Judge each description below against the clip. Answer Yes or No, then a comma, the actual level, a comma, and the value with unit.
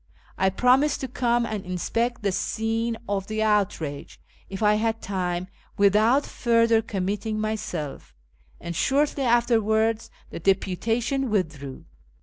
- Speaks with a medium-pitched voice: No, high, 215 Hz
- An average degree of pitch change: Yes, average, 3.4 semitones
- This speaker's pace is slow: Yes, slow, 125 wpm